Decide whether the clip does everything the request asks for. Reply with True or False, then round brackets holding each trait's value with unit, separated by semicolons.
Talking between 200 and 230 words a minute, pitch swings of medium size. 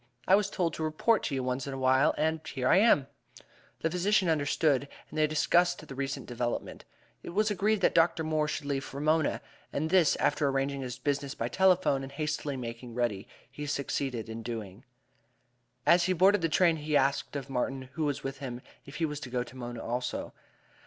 True (205 wpm; 3.9 semitones)